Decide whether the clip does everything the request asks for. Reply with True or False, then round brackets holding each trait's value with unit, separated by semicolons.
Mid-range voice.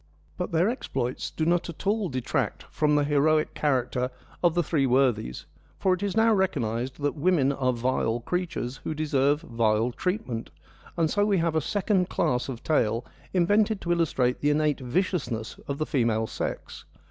True (150 Hz)